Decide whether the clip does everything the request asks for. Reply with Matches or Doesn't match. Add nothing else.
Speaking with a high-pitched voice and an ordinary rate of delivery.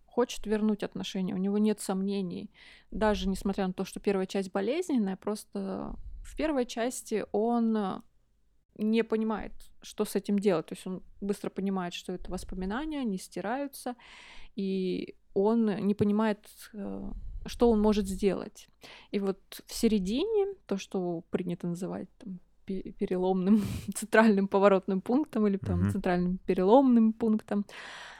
Matches